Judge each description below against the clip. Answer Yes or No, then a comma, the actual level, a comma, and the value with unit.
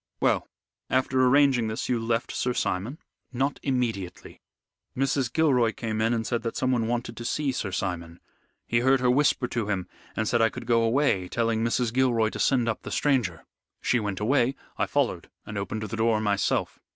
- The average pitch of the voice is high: No, low, 115 Hz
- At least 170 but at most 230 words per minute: Yes, average, 190 wpm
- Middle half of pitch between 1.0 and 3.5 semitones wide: Yes, average, 2.9 semitones